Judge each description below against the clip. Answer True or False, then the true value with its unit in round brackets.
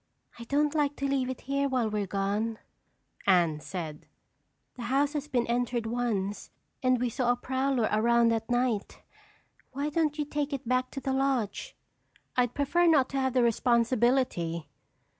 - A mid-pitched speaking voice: False (250 Hz)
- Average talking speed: True (165 wpm)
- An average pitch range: True (3.4 semitones)